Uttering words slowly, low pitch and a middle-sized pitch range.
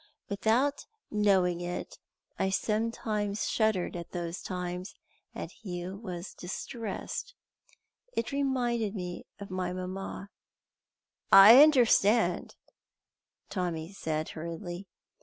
No: slow, 95 wpm; high, 195 Hz; average, 3.8 semitones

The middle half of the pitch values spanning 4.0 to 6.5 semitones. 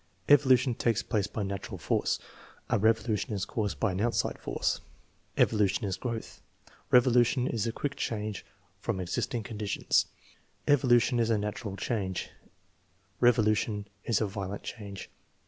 No: average, 2.8 semitones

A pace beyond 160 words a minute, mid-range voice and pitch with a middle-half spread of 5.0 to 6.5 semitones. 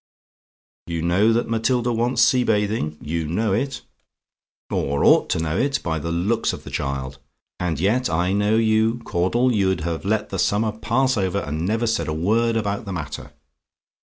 No: average, 180 wpm; low, 100 Hz; wide, 5.5 semitones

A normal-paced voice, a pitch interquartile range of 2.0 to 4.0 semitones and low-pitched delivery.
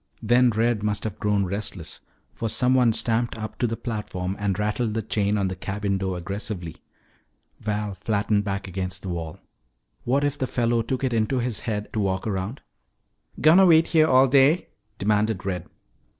Yes: average, 175 wpm; average, 3.5 semitones; low, 105 Hz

